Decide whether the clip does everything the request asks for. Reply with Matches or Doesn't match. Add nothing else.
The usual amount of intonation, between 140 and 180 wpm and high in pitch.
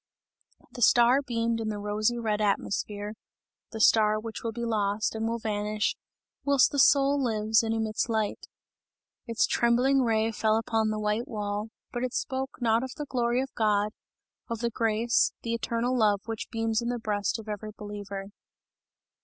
Doesn't match